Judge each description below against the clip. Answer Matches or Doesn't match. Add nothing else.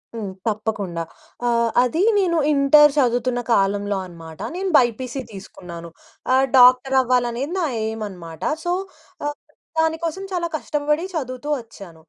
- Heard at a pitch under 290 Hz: Matches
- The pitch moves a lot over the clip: Matches